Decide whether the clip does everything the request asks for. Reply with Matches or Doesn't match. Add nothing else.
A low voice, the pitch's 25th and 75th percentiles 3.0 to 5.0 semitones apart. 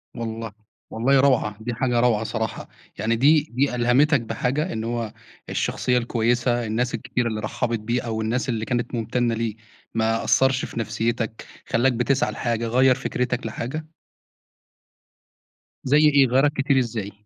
Doesn't match